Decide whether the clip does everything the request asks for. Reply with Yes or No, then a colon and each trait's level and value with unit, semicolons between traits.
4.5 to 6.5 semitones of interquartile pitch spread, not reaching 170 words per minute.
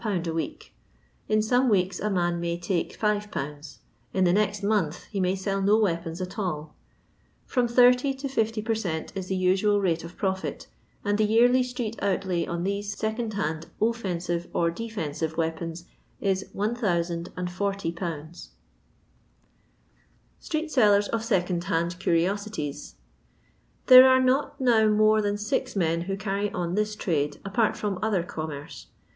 No: average, 4.0 semitones; average, 150 wpm